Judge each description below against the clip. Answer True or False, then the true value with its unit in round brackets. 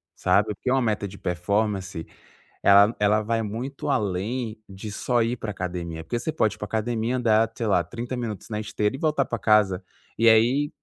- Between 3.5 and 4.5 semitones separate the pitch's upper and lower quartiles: False (2.8 semitones)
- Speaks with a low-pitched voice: True (110 Hz)